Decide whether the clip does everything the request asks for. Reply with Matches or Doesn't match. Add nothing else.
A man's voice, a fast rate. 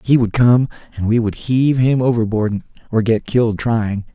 Doesn't match